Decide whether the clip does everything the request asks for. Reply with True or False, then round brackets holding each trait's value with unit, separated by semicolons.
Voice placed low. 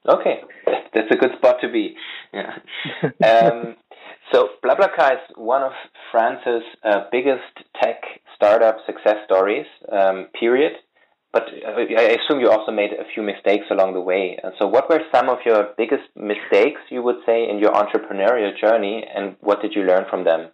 True (115 Hz)